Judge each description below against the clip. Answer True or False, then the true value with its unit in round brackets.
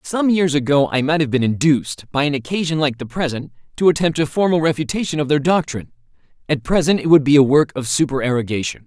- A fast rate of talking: True (210 wpm)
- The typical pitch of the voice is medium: True (145 Hz)